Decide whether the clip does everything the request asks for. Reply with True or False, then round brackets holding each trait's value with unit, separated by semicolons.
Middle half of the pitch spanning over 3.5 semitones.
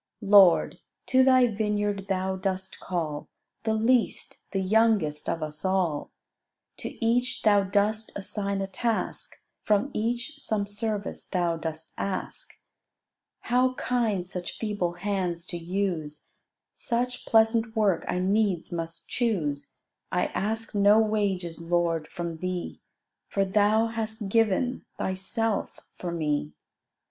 True (4.0 semitones)